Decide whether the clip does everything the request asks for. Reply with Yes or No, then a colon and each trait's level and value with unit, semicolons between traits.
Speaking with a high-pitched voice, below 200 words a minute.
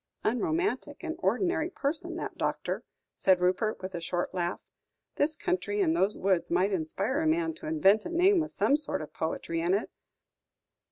Yes: very high, 260 Hz; average, 175 wpm